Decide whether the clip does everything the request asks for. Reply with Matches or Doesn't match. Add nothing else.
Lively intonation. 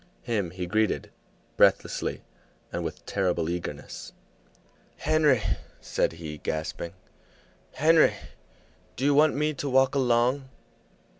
Matches